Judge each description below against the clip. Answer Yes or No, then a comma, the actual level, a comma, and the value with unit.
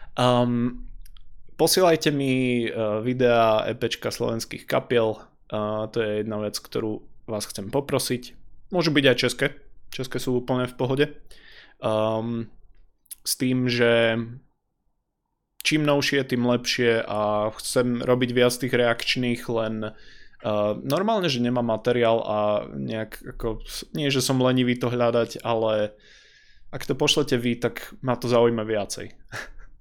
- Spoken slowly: No, average, 130 wpm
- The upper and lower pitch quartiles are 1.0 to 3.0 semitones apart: Yes, average, 2.7 semitones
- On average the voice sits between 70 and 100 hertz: No, low, 120 Hz